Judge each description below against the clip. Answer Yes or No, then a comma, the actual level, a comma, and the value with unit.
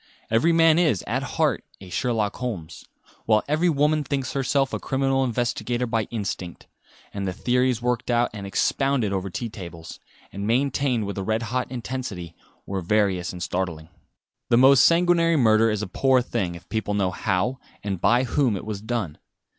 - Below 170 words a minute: No, average, 175 wpm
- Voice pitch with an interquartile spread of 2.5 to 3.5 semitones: No, average, 5.0 semitones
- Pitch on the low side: Yes, low, 115 Hz